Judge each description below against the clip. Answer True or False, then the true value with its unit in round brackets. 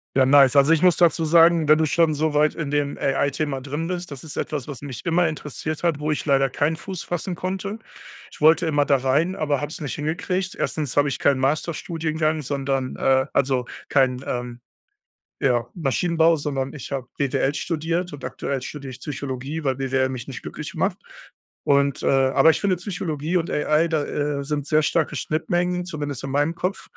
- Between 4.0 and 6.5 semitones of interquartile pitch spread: False (3.2 semitones)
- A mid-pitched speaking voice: True (150 Hz)